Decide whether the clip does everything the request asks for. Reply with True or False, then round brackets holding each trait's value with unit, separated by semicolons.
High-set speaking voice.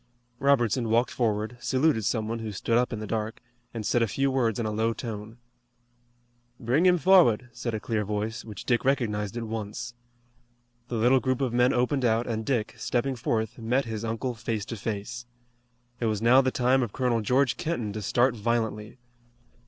False (115 Hz)